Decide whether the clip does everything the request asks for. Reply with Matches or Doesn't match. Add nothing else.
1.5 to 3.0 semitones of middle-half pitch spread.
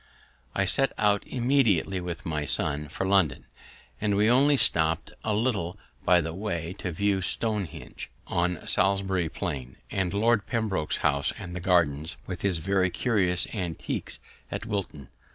Doesn't match